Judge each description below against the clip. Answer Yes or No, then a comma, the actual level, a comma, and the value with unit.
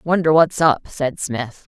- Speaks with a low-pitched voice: No, medium, 150 Hz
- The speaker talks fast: No, average, 170 wpm